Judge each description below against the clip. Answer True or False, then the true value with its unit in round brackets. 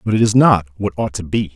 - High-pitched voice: False (100 Hz)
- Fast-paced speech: True (310 wpm)